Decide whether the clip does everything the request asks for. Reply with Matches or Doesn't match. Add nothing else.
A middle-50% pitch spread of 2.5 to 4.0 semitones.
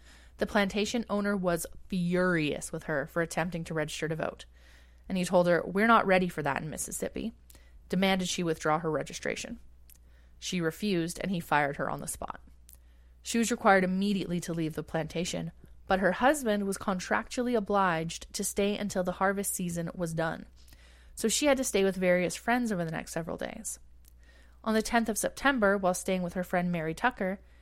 Doesn't match